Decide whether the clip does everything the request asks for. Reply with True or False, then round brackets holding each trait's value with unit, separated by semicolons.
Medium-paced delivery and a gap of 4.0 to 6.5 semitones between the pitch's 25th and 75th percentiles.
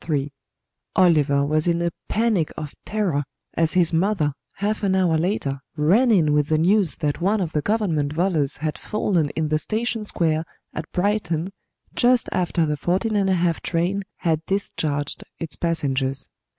True (155 wpm; 4.5 semitones)